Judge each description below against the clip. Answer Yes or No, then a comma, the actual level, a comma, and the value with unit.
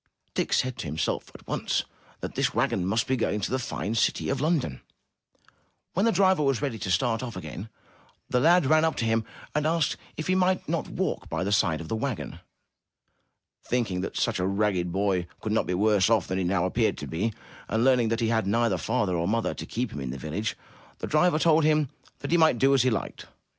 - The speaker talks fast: Yes, fast, 225 wpm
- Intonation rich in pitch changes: Yes, wide, 6.4 semitones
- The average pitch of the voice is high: No, low, 115 Hz